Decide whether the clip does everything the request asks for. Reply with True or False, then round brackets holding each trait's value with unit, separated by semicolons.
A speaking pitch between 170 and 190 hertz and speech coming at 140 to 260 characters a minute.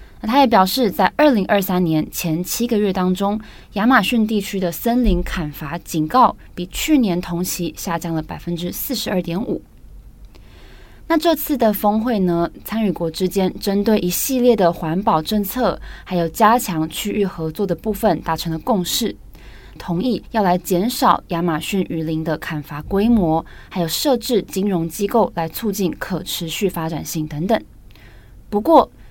True (185 Hz; 245 characters per minute)